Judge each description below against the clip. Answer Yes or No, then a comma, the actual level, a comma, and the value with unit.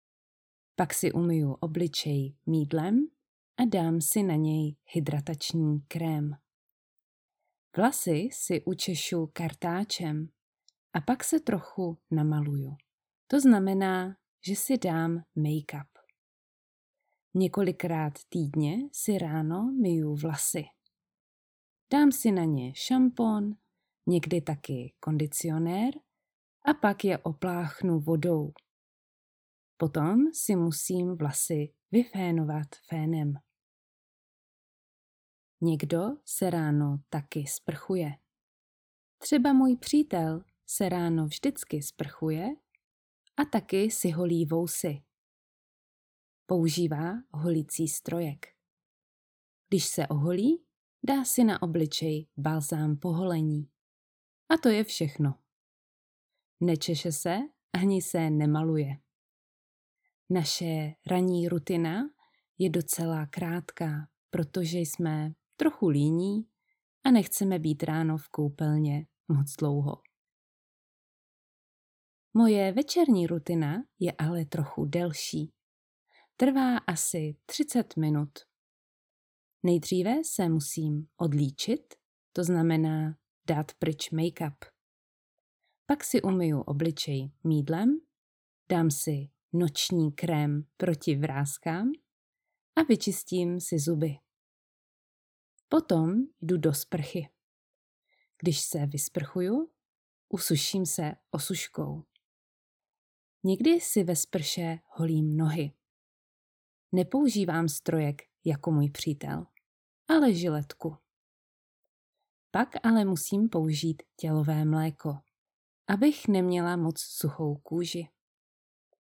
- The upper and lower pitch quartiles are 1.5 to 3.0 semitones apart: No, average, 3.9 semitones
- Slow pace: Yes, slow, 90 wpm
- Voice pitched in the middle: Yes, medium, 165 Hz